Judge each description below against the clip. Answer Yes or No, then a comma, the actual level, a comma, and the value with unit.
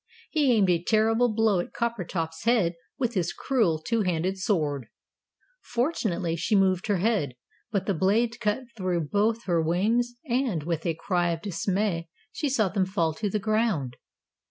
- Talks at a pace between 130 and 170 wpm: Yes, average, 165 wpm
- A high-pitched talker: Yes, high, 195 Hz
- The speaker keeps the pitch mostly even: No, average, 4.9 semitones